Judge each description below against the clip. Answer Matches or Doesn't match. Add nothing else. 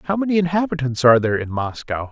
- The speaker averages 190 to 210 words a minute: Matches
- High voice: Doesn't match